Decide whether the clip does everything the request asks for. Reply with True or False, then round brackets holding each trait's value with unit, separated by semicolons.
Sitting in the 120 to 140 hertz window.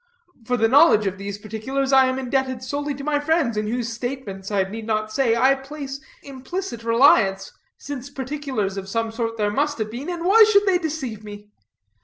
False (255 Hz)